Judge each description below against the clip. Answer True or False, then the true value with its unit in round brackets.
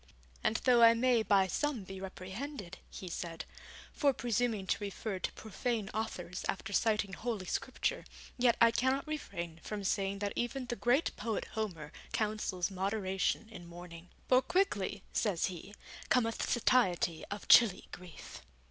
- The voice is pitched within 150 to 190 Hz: False (210 Hz)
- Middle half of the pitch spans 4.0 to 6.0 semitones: True (4.3 semitones)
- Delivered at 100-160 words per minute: True (150 wpm)